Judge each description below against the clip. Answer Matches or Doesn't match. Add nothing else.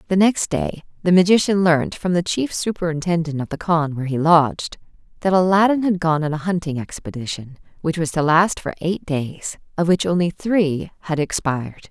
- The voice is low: Doesn't match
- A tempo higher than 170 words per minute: Matches